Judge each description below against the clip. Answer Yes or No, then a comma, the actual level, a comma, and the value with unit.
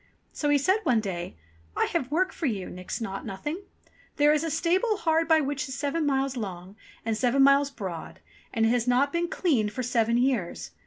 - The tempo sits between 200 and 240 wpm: Yes, fast, 205 wpm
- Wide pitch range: Yes, wide, 5.7 semitones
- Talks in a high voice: Yes, very high, 270 Hz